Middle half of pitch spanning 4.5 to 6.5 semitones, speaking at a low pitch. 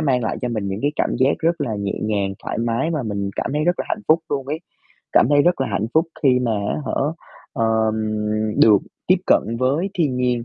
Yes: average, 5.1 semitones; low, 125 Hz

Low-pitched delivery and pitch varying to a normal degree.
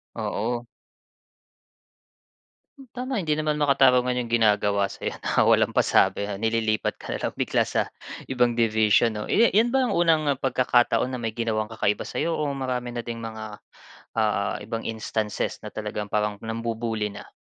Yes: low, 115 Hz; average, 3.4 semitones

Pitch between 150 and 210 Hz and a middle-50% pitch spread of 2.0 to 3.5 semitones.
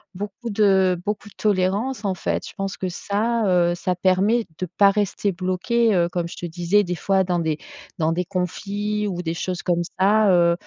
Yes: high, 190 Hz; average, 2.7 semitones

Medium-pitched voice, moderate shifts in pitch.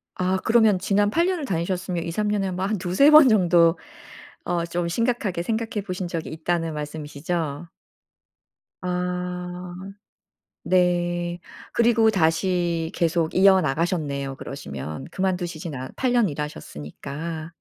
Yes: medium, 175 Hz; average, 3.0 semitones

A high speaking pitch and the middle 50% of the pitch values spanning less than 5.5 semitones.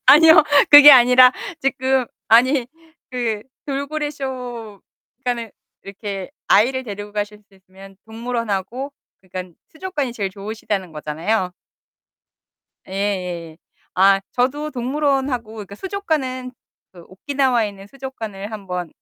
Yes: high, 230 Hz; average, 5.1 semitones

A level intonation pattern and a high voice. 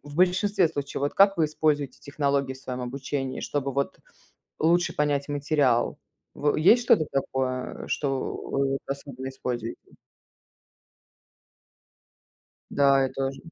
No: narrow, 2.2 semitones; medium, 140 Hz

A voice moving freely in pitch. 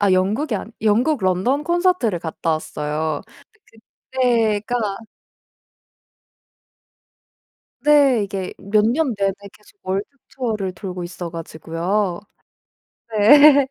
Yes: wide, 5.7 semitones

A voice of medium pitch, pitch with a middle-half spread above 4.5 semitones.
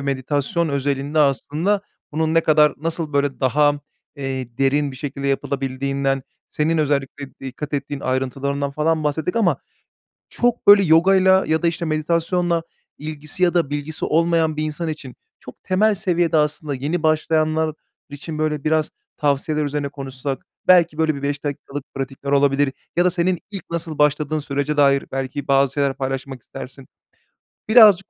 No: medium, 150 Hz; average, 2.7 semitones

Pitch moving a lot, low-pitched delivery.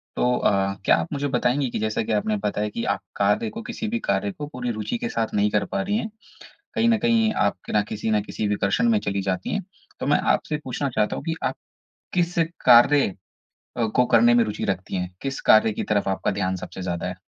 Yes: wide, 6.1 semitones; low, 110 Hz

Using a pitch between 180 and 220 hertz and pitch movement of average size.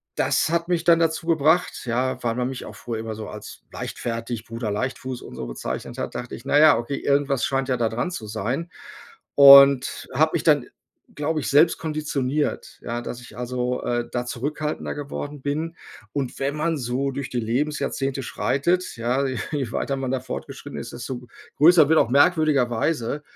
No: low, 135 Hz; average, 3.7 semitones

